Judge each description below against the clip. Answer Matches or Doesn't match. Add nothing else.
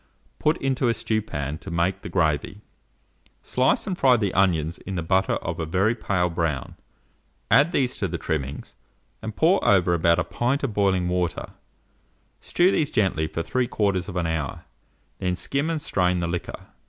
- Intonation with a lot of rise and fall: Matches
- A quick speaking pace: Doesn't match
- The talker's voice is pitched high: Doesn't match